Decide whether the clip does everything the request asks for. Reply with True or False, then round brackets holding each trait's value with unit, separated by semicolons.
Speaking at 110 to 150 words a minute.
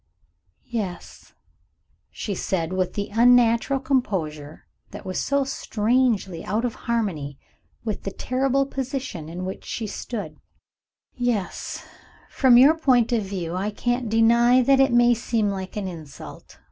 True (135 wpm)